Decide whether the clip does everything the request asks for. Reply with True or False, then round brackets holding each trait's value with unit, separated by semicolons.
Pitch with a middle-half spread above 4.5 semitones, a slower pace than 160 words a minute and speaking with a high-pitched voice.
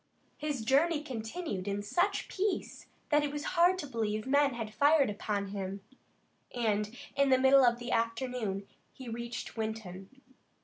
True (5.2 semitones; 150 wpm; 240 Hz)